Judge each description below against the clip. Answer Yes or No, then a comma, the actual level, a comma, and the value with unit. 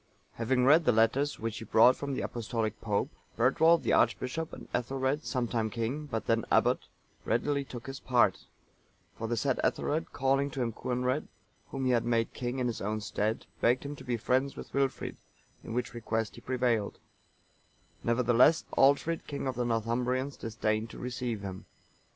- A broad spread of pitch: No, average, 2.9 semitones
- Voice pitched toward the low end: Yes, low, 125 Hz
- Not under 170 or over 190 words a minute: Yes, average, 175 wpm